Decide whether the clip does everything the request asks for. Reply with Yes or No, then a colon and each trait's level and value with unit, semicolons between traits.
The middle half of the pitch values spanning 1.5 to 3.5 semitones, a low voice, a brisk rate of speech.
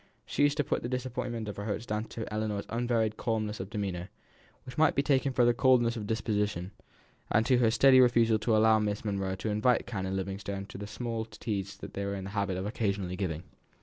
Yes: average, 3.0 semitones; low, 110 Hz; fast, 215 wpm